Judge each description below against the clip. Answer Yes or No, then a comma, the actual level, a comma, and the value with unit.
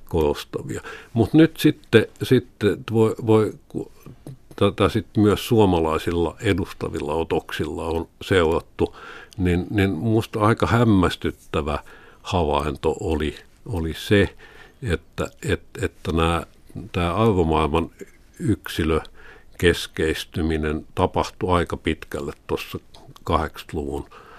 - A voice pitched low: Yes, very low, 95 Hz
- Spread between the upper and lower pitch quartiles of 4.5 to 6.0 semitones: Yes, average, 4.9 semitones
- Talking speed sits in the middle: No, slow, 90 wpm